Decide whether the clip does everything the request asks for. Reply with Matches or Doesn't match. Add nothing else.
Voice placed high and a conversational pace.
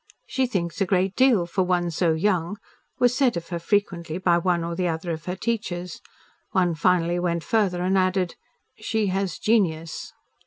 Doesn't match